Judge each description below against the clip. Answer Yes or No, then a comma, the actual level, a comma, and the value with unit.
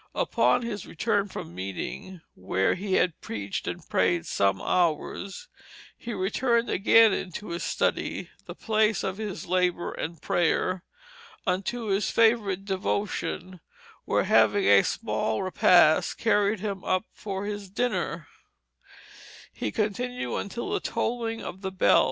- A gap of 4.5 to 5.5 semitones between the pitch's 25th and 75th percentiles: No, average, 3.5 semitones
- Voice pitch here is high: Yes, high, 195 Hz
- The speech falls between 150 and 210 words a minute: No, slow, 135 wpm